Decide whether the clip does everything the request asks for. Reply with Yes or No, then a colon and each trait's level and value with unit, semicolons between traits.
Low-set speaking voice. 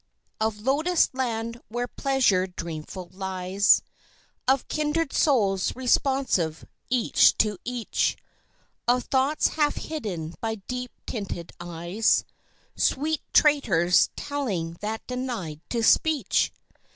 No: high, 230 Hz